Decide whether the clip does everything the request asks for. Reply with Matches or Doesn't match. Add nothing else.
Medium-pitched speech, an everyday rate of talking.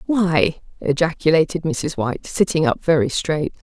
Doesn't match